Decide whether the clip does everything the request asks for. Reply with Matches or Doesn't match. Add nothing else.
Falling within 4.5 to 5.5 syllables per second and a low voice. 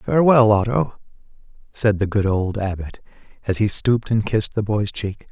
Matches